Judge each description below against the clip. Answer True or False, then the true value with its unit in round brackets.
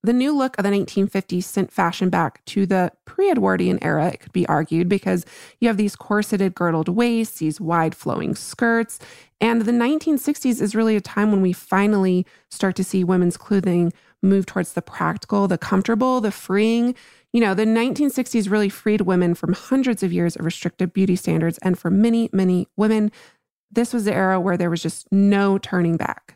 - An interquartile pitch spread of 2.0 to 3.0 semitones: False (4.0 semitones)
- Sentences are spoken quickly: False (185 wpm)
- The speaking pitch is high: True (195 Hz)